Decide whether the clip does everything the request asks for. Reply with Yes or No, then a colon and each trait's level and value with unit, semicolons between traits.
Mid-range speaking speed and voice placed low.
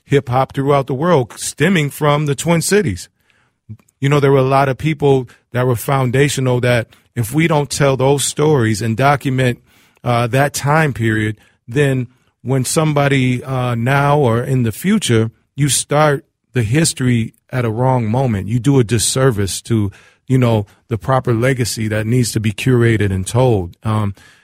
Yes: average, 170 wpm; low, 130 Hz